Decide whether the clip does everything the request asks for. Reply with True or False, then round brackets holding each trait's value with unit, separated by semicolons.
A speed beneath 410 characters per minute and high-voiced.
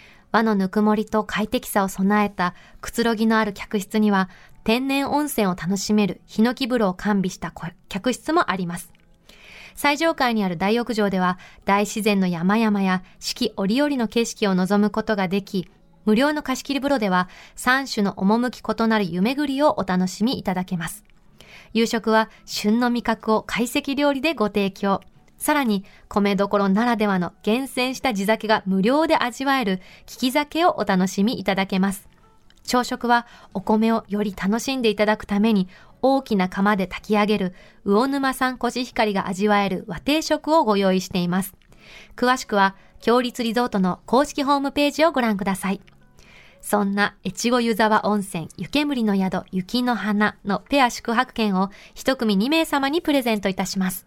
True (320 characters per minute; 215 Hz)